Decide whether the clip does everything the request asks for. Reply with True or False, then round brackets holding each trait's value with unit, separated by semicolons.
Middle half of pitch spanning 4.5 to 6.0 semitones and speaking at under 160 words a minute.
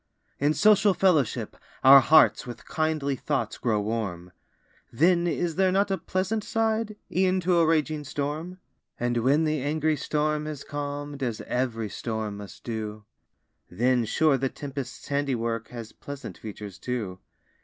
True (5.4 semitones; 145 wpm)